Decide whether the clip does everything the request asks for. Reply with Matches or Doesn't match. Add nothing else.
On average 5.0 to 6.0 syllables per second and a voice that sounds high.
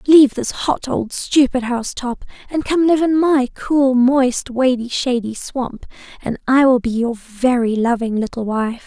Doesn't match